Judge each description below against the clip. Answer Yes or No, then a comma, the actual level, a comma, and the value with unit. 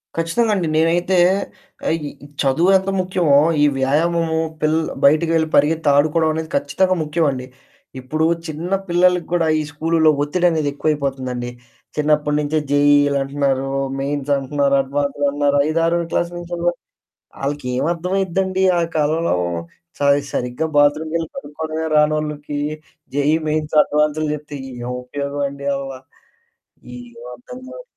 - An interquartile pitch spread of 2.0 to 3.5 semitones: Yes, average, 2.7 semitones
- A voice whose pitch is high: No, medium, 150 Hz